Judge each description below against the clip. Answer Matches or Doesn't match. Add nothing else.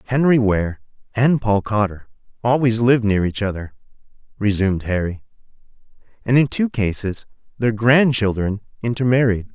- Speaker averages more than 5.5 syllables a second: Doesn't match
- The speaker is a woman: Doesn't match